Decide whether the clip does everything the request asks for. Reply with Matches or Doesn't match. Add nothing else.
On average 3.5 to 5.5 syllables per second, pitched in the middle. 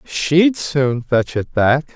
Doesn't match